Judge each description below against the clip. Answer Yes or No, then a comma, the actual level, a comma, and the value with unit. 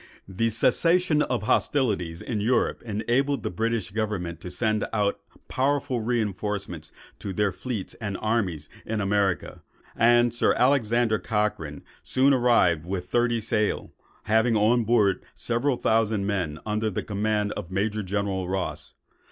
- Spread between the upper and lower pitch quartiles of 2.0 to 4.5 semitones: Yes, average, 3.4 semitones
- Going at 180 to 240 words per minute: No, slow, 135 wpm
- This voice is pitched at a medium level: No, low, 110 Hz